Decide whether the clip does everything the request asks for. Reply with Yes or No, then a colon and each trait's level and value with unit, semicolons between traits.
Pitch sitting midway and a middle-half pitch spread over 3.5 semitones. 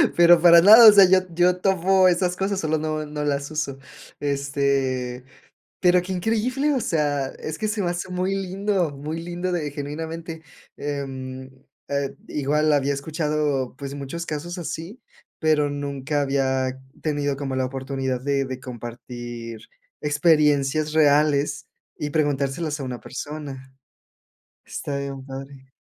Yes: medium, 150 Hz; average, 3.9 semitones